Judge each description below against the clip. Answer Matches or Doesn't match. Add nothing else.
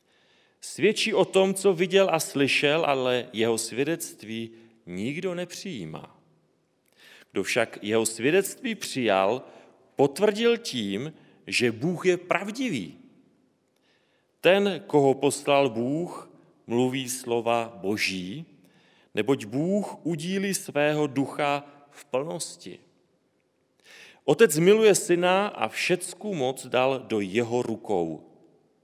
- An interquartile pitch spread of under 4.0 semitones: Doesn't match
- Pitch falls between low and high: Matches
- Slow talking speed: Matches